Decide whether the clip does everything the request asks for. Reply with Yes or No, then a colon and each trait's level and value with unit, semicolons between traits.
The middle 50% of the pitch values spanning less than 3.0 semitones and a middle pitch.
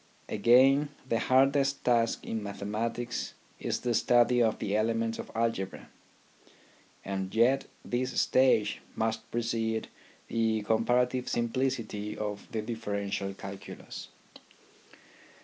No: narrow, 2.5 semitones; low, 115 Hz